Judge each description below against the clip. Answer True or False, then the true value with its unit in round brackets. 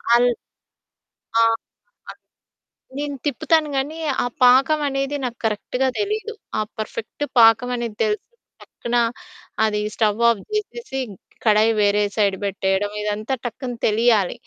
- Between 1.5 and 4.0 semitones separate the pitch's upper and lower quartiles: False (4.4 semitones)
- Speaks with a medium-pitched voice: False (235 Hz)